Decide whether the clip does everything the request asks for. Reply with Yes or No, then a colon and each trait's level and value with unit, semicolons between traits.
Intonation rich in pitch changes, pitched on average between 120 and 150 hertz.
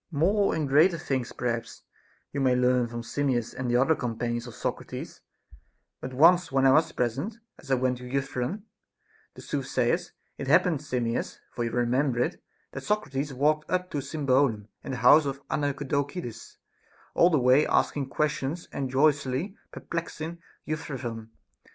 No: average, 3.6 semitones; low, 135 Hz